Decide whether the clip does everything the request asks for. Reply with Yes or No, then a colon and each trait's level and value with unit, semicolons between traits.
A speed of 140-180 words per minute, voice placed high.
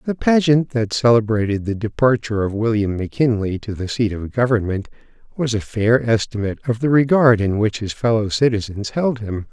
No: average, 175 wpm; low, 115 Hz